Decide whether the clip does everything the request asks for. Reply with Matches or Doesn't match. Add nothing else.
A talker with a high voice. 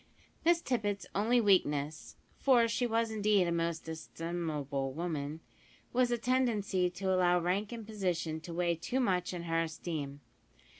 Doesn't match